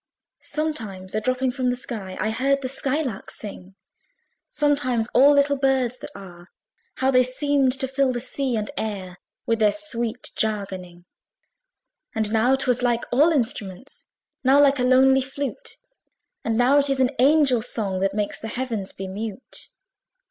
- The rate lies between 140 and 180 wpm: Yes, average, 165 wpm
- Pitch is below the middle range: No, very high, 250 Hz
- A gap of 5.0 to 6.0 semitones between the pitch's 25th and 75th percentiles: No, average, 3.9 semitones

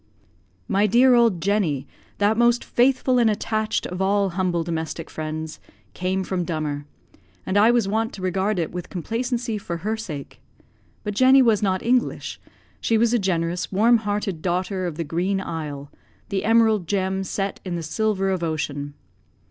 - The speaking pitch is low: No, high, 195 Hz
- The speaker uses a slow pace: No, average, 165 wpm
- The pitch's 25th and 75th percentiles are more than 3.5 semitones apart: Yes, average, 4.5 semitones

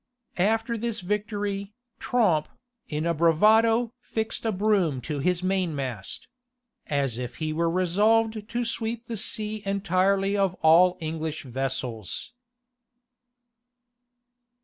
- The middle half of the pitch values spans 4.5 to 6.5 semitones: Yes, wide, 5.4 semitones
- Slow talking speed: Yes, slow, 110 wpm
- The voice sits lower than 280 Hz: Yes, high, 190 Hz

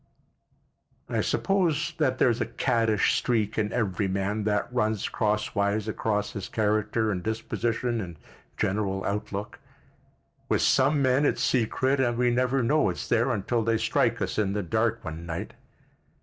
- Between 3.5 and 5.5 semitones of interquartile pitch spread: No, average, 3.1 semitones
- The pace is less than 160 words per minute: Yes, average, 150 wpm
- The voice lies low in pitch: Yes, low, 110 Hz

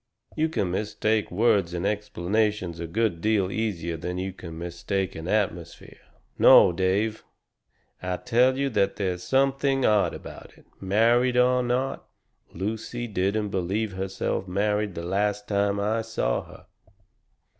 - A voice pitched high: No, low, 100 Hz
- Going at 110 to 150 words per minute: Yes, average, 140 wpm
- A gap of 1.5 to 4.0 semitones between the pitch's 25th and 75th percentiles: Yes, average, 3.4 semitones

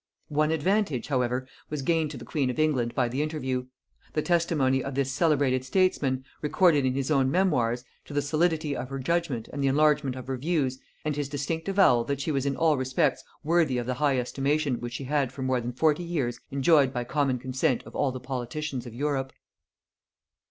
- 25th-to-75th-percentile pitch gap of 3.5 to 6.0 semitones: No, average, 2.9 semitones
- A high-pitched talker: No, medium, 140 Hz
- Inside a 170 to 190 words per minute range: No, average, 200 wpm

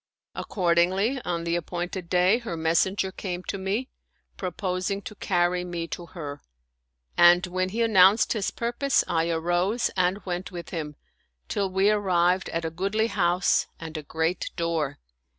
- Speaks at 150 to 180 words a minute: Yes, average, 155 wpm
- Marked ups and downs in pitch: No, narrow, 2.4 semitones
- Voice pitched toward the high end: No, medium, 180 Hz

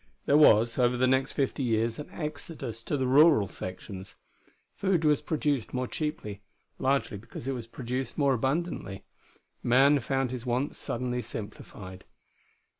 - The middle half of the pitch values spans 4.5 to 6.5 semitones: No, average, 3.8 semitones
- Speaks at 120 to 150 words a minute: Yes, average, 145 wpm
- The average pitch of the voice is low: Yes, low, 130 Hz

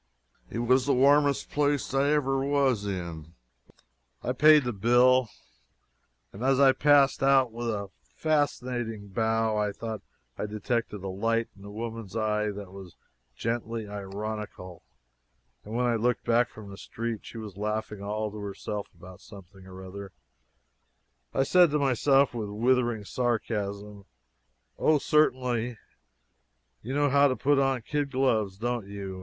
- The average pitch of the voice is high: No, low, 115 Hz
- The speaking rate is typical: Yes, average, 150 wpm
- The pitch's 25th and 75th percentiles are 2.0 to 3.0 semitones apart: No, average, 4.4 semitones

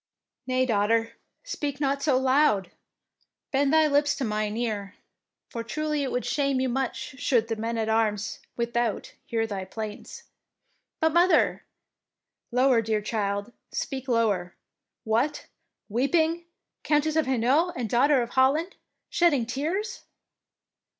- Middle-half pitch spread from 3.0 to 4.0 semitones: No, average, 4.5 semitones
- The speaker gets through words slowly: No, average, 145 wpm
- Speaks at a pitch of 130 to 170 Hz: No, very high, 255 Hz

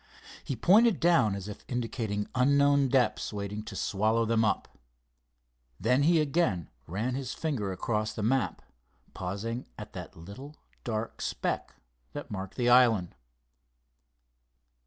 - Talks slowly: Yes, slow, 130 wpm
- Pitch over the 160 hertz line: No, low, 115 Hz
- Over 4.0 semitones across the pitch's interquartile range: Yes, average, 4.6 semitones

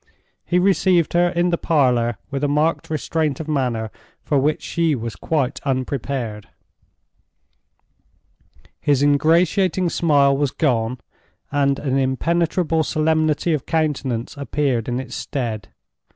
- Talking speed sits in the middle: No, slow, 125 wpm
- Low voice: No, medium, 145 Hz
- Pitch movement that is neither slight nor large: Yes, average, 3.8 semitones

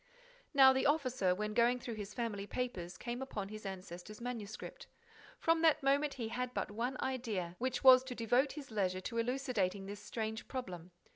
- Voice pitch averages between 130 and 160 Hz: No, high, 235 Hz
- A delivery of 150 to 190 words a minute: Yes, average, 180 wpm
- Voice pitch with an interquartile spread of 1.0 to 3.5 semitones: No, average, 4.1 semitones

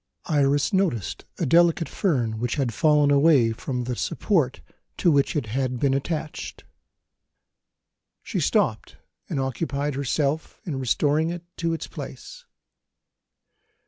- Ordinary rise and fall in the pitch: Yes, average, 3.9 semitones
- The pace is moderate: No, slow, 125 wpm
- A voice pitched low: No, medium, 145 Hz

